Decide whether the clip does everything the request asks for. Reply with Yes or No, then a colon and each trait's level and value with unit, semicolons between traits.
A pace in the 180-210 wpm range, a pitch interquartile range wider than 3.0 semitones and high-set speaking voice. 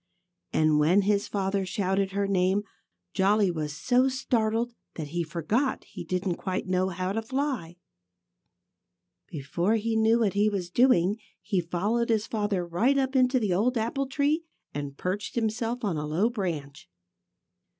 No: average, 155 wpm; average, 4.6 semitones; high, 200 Hz